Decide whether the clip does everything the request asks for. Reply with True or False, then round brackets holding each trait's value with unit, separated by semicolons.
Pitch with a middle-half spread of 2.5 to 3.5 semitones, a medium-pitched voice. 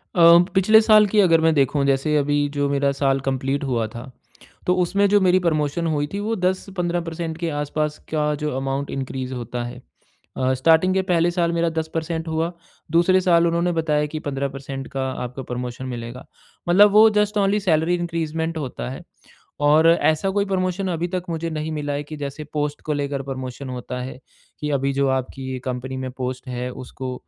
False (4.3 semitones; 150 Hz)